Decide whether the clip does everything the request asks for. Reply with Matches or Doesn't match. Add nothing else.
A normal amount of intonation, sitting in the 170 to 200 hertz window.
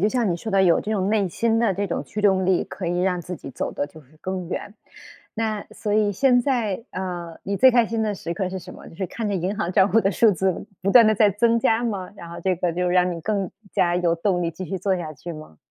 Matches